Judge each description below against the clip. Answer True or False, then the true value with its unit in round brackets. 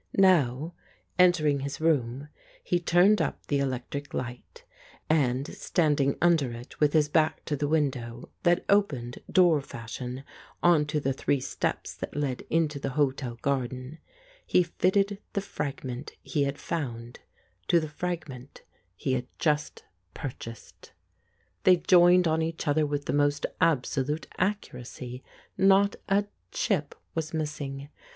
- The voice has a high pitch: False (145 Hz)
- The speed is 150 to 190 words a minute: False (140 wpm)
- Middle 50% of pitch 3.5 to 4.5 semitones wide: True (4.2 semitones)